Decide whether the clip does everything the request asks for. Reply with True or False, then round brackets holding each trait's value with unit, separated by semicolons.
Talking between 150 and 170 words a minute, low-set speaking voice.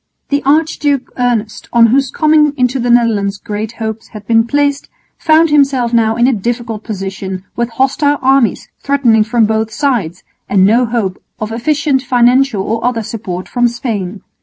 False (160 wpm; 235 Hz)